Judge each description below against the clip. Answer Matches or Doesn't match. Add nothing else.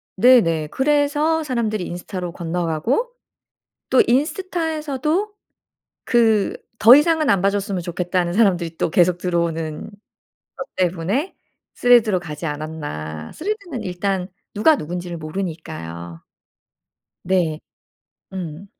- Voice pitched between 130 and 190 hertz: Matches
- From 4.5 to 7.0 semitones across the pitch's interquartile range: Doesn't match